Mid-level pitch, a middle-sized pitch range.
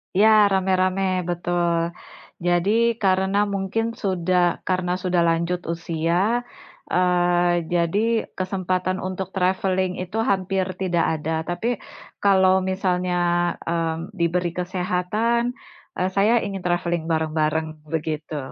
No: medium, 180 Hz; narrow, 1.8 semitones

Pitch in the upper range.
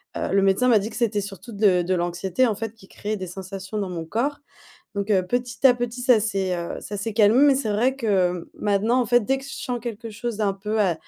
Yes: high, 210 Hz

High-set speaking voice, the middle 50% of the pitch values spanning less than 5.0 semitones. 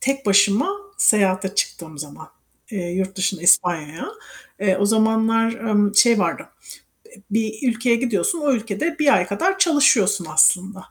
Yes: high, 205 Hz; average, 3.6 semitones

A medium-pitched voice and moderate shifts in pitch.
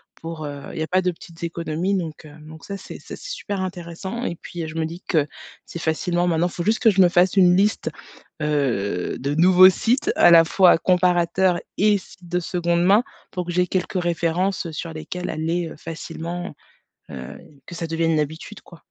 No: medium, 175 Hz; narrow, 2.2 semitones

